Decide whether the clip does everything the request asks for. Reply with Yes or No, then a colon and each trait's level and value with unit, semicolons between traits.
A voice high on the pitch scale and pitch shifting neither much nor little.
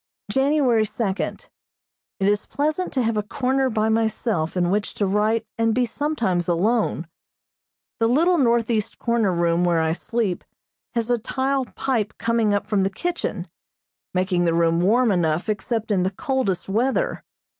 Yes: high, 220 Hz; average, 4.5 semitones